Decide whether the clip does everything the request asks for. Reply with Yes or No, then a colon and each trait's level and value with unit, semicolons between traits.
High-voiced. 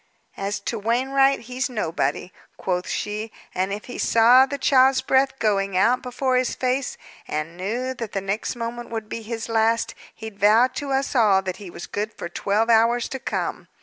Yes: high, 230 Hz